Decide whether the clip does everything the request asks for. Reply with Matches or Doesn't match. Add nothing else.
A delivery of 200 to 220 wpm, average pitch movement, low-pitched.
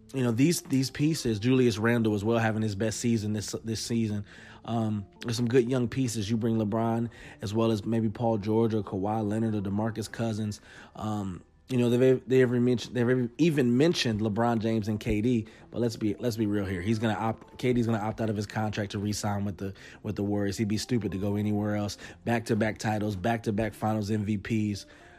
Doesn't match